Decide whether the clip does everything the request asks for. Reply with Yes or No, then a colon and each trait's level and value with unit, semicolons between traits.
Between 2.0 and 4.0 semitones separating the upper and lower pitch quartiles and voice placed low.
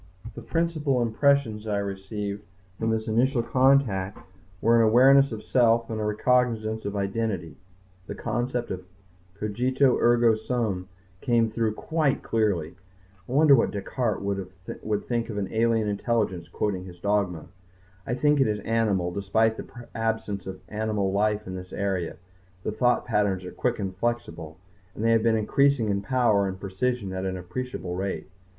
Yes: average, 3.3 semitones; low, 110 Hz